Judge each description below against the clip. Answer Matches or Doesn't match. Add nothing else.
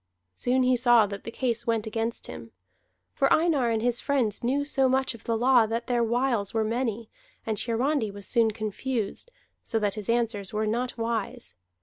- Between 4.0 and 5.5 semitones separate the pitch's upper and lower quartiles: Doesn't match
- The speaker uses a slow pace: Doesn't match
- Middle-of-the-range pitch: Doesn't match